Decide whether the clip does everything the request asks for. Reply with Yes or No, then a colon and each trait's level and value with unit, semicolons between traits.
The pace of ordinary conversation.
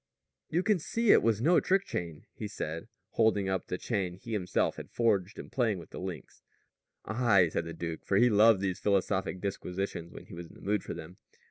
No: fast, 215 wpm